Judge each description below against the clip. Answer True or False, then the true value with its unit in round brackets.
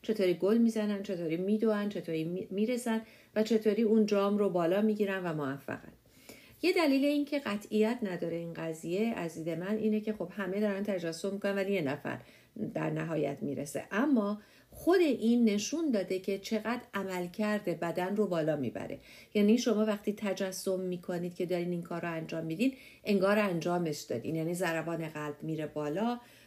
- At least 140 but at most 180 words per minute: True (165 wpm)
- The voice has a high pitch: True (195 Hz)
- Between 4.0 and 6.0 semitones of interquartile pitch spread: True (4.3 semitones)